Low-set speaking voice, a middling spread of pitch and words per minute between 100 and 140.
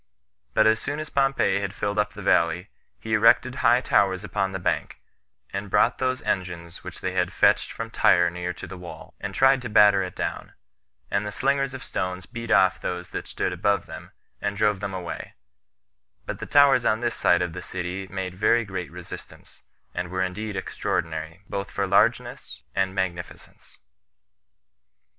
No: low, 100 Hz; average, 3.5 semitones; average, 180 wpm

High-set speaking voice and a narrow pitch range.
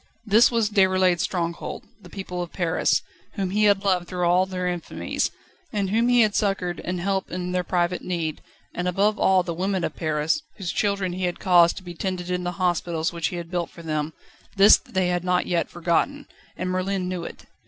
No: medium, 180 Hz; narrow, 1.9 semitones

